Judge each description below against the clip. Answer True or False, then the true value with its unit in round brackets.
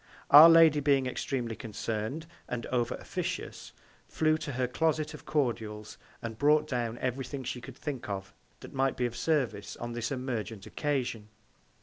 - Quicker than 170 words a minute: False (160 wpm)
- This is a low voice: True (125 Hz)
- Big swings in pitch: False (4.0 semitones)